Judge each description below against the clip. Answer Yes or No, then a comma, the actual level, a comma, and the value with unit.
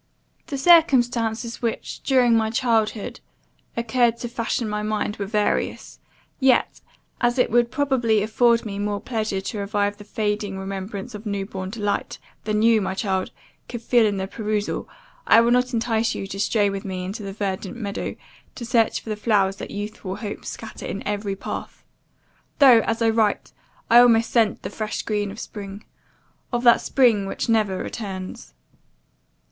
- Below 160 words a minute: No, average, 165 wpm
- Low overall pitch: No, high, 215 Hz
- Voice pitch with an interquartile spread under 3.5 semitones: Yes, narrow, 2.6 semitones